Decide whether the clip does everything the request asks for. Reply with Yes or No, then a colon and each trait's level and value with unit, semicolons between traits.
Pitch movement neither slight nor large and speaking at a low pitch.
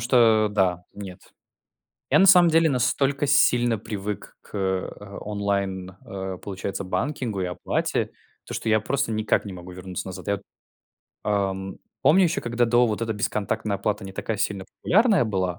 Yes: average, 4.0 semitones; low, 105 Hz